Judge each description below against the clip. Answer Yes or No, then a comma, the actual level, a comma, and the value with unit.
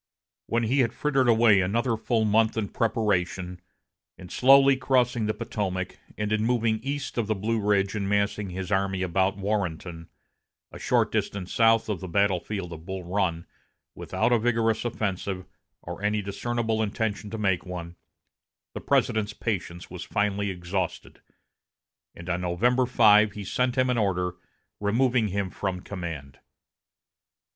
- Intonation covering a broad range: No, average, 3.4 semitones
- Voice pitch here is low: Yes, low, 105 Hz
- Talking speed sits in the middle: Yes, average, 150 wpm